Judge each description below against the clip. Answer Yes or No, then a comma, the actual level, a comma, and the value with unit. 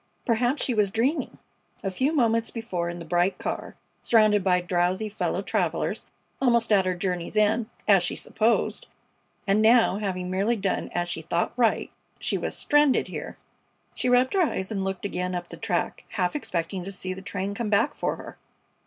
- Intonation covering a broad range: No, average, 4.0 semitones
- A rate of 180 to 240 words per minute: Yes, average, 185 wpm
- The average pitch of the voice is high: Yes, high, 200 Hz